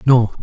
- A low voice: Yes, low, 120 Hz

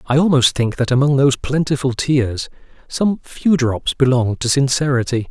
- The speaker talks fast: No, average, 160 wpm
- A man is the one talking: Yes, male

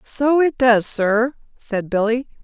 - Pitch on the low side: No, high, 240 Hz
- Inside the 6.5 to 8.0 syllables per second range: No, 3.5 syllables/s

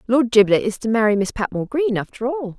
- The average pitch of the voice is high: Yes, high, 230 Hz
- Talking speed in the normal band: No, fast, 230 wpm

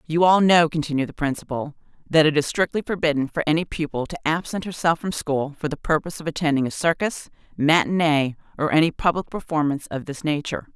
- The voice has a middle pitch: Yes, medium, 155 Hz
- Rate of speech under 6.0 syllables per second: No, 6.1 syllables/s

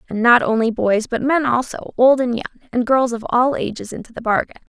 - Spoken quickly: Yes, fast, 225 wpm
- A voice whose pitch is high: Yes, high, 240 Hz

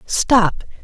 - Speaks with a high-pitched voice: Yes, high, 210 Hz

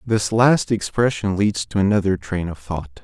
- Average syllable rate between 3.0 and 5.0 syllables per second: Yes, 4.5 syllables/s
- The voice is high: No, low, 100 Hz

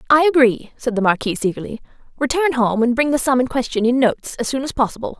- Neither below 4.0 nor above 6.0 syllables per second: No, 6.6 syllables/s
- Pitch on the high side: Yes, very high, 250 Hz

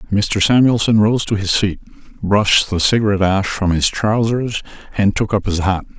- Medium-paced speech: Yes, average, 180 wpm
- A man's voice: Yes, male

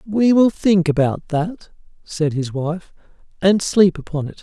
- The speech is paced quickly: No, average, 165 wpm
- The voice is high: No, medium, 175 Hz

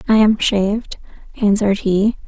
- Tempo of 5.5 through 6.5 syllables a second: No, 4.9 syllables/s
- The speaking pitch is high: Yes, high, 205 Hz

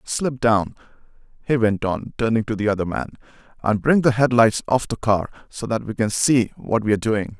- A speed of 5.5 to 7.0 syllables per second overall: No, 5.1 syllables/s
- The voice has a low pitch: Yes, low, 115 Hz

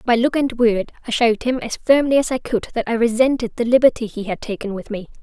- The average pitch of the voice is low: No, high, 235 Hz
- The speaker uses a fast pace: Yes, fast, 255 wpm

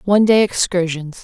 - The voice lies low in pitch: No, medium, 185 Hz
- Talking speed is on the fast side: No, average, 145 wpm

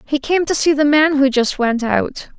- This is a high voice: Yes, very high, 280 Hz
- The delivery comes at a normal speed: No, fast, 250 wpm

